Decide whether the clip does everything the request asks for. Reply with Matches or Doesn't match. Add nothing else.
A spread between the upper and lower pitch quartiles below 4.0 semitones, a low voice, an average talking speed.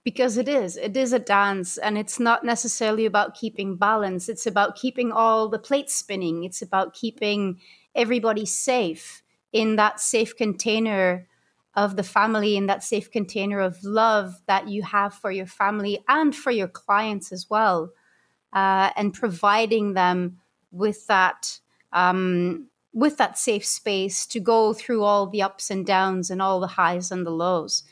Doesn't match